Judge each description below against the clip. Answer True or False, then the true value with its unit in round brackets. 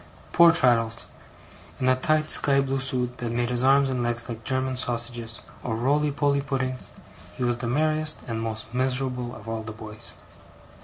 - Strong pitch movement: False (2.6 semitones)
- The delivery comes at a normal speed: True (175 wpm)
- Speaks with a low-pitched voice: True (125 Hz)